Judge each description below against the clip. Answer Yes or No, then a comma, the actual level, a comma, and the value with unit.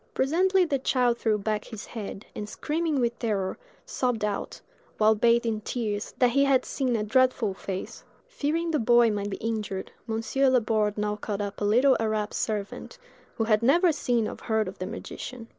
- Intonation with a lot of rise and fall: No, average, 3.6 semitones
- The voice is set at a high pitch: Yes, high, 225 Hz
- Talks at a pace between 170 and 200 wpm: Yes, average, 185 wpm